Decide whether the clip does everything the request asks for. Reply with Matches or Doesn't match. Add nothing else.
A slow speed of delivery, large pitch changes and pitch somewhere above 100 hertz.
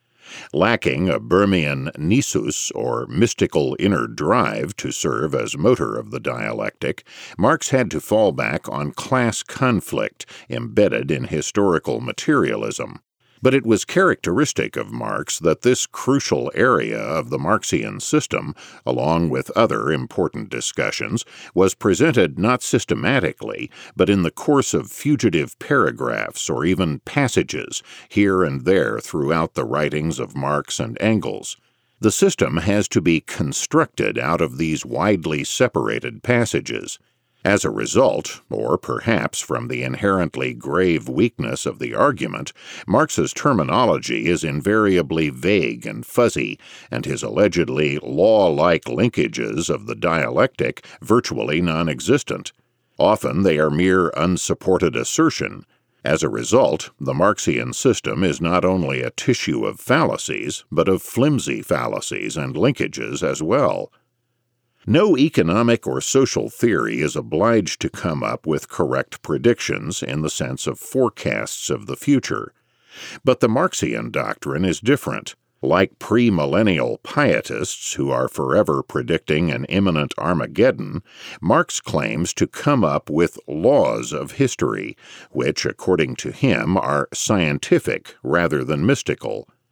Doesn't match